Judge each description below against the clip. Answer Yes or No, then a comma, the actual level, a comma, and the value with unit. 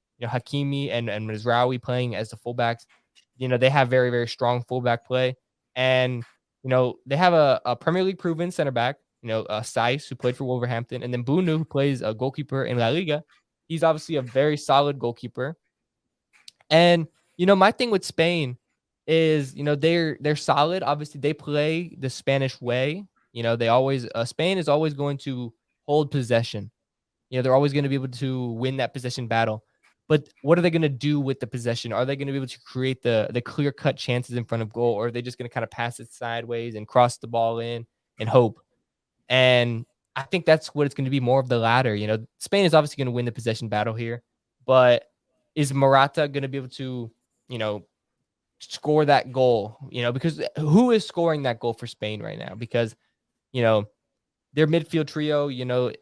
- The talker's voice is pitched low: Yes, low, 130 Hz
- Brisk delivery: Yes, fast, 215 wpm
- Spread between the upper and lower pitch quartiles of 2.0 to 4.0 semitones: Yes, average, 3.6 semitones